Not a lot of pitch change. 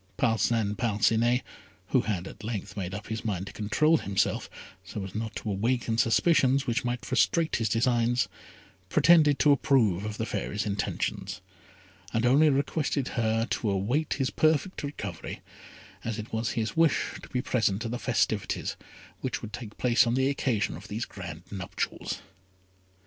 No: average, 4.0 semitones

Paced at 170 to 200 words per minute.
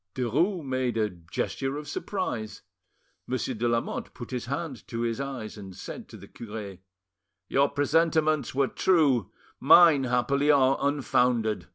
No: average, 145 wpm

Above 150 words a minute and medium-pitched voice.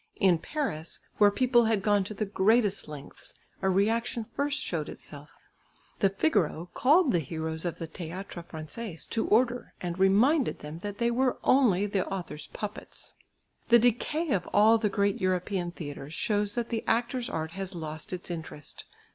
No: average, 165 wpm; high, 200 Hz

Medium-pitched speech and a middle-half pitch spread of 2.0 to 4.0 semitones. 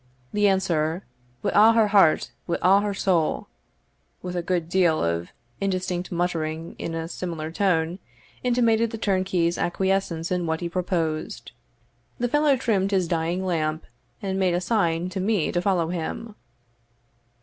Yes: medium, 180 Hz; average, 3.0 semitones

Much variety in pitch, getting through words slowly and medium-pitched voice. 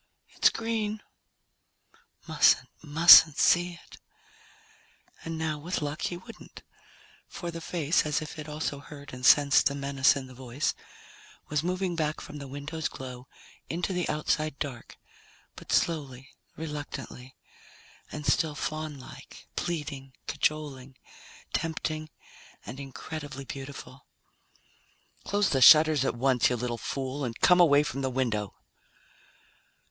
No: average, 3.1 semitones; slow, 130 wpm; medium, 145 Hz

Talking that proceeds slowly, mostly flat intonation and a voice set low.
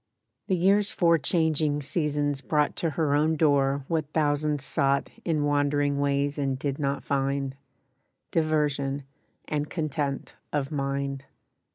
No: slow, 130 wpm; narrow, 1.9 semitones; medium, 145 Hz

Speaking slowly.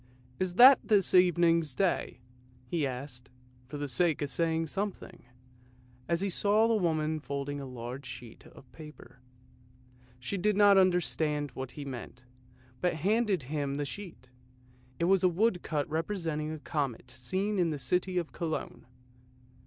No: average, 155 wpm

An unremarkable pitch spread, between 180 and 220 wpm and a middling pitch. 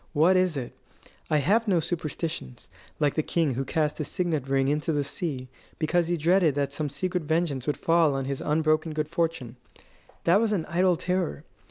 Yes: average, 3.3 semitones; average, 190 wpm; medium, 155 Hz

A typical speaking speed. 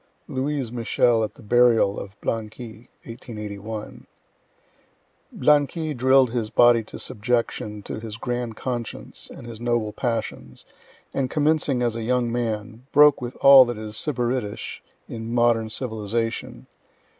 No: slow, 130 wpm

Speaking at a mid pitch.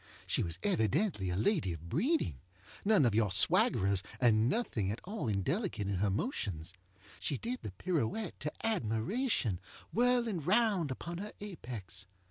No: low, 125 Hz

